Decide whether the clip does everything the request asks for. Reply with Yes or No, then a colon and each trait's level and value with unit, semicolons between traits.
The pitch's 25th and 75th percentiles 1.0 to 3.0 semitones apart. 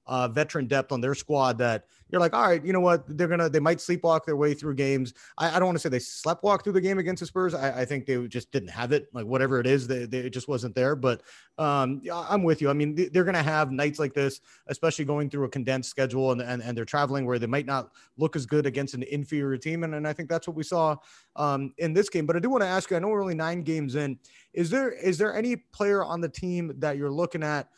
No: average, 4.2 semitones